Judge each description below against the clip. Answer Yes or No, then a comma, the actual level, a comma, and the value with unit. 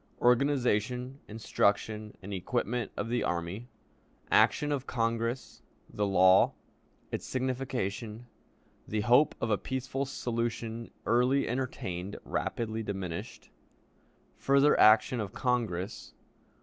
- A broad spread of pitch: No, average, 3.4 semitones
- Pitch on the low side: Yes, low, 115 Hz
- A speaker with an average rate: No, slow, 100 wpm